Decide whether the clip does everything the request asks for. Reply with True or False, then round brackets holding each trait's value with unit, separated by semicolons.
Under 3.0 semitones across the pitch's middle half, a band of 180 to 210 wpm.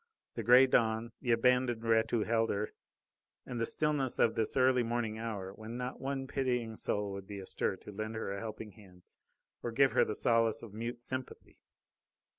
True (2.4 semitones; 190 wpm)